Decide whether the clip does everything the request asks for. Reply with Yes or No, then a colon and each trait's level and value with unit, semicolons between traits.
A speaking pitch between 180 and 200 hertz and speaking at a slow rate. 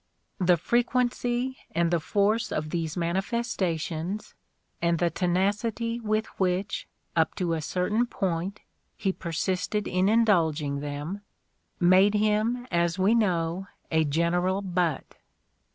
Yes: medium, 185 Hz; slow, 120 wpm